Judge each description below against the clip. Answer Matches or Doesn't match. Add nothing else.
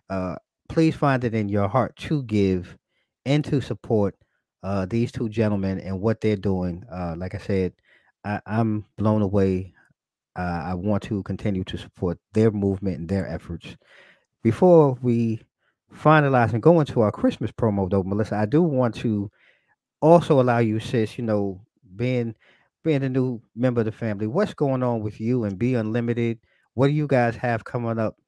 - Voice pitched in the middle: Doesn't match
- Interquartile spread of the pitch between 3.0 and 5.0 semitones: Matches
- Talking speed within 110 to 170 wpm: Doesn't match